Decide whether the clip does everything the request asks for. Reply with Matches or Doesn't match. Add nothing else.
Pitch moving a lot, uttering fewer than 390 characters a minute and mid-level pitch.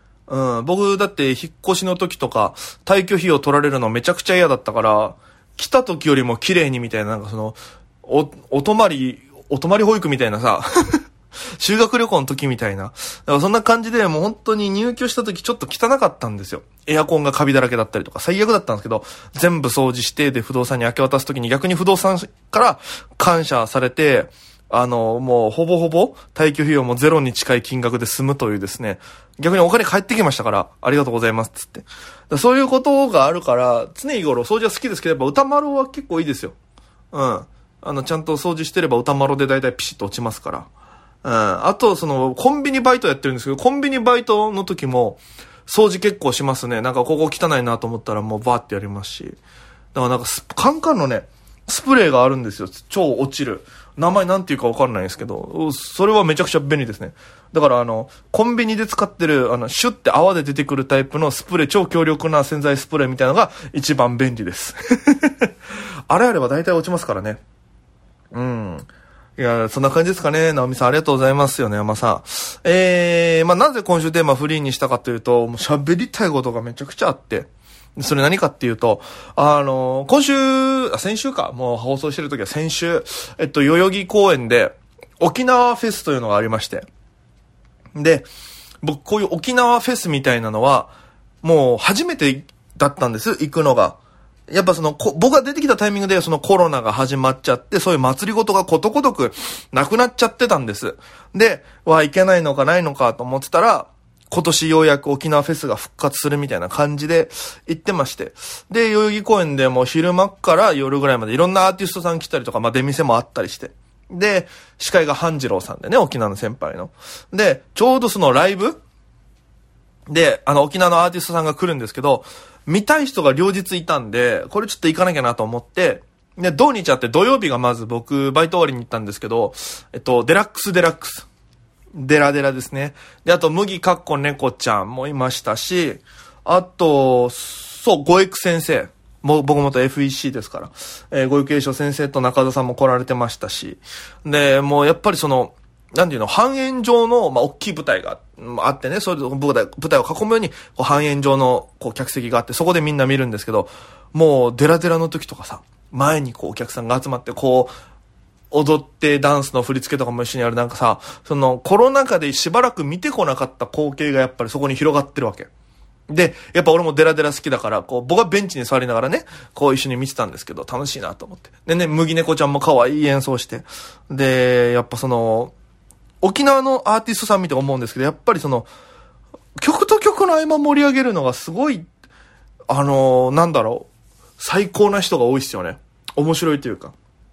Doesn't match